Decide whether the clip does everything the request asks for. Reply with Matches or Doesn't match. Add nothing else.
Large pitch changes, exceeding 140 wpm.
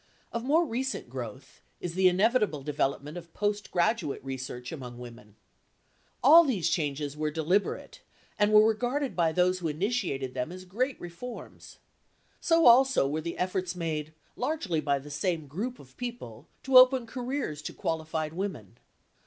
Matches